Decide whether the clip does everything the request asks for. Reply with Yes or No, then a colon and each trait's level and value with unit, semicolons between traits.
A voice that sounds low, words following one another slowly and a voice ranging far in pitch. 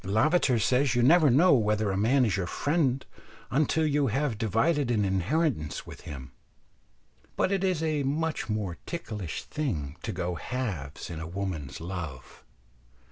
No: low, 115 Hz; average, 155 wpm; wide, 7.9 semitones